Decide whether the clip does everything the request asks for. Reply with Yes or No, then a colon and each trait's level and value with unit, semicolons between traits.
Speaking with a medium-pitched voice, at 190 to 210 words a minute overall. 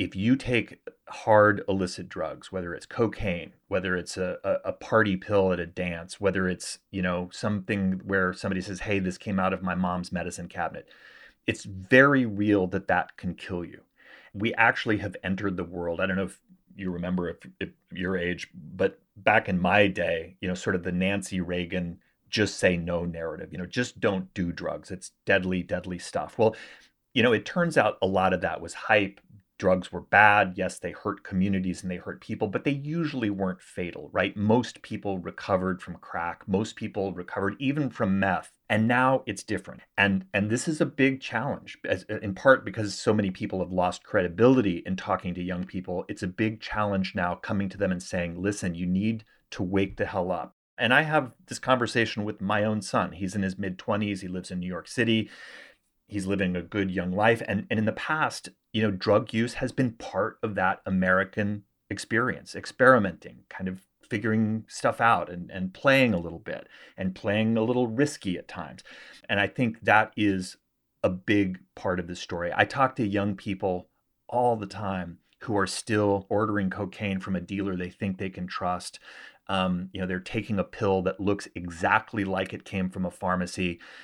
No: very low, 95 Hz; average, 200 wpm